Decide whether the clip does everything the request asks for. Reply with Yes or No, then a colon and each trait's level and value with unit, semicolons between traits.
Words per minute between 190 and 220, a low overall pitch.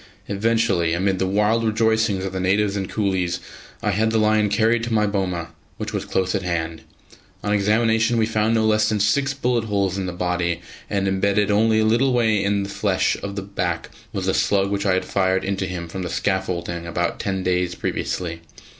Yes: fast, 205 wpm; low, 100 Hz